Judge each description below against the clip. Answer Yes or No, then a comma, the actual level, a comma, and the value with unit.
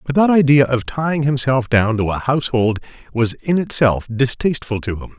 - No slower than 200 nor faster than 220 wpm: No, average, 185 wpm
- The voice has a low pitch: Yes, low, 130 Hz